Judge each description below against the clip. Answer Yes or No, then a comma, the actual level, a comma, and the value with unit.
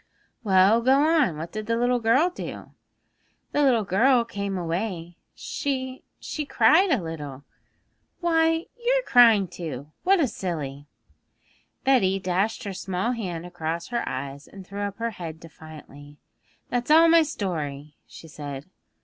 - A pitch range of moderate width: No, wide, 7.9 semitones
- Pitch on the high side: Yes, high, 200 Hz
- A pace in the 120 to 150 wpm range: Yes, average, 145 wpm